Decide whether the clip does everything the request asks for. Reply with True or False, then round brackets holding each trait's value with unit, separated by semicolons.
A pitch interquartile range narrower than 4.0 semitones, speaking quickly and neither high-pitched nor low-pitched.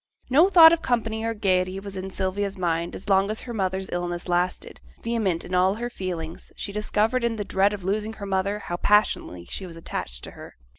False (3.0 semitones; 210 wpm; 195 Hz)